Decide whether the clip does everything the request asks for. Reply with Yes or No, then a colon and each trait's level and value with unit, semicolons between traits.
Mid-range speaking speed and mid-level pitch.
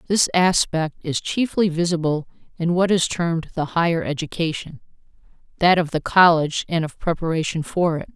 Yes: average, 145 wpm; medium, 165 Hz